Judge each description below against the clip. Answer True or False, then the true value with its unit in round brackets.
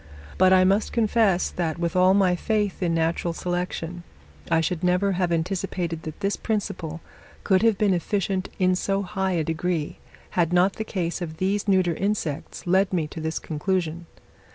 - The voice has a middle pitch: True (180 Hz)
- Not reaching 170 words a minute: False (175 wpm)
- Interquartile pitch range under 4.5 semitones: True (2.6 semitones)